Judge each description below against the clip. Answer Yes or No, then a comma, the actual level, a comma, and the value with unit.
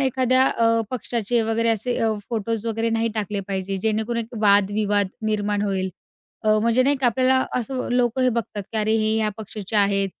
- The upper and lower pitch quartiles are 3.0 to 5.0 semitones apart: No, narrow, 2.5 semitones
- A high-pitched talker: Yes, high, 220 Hz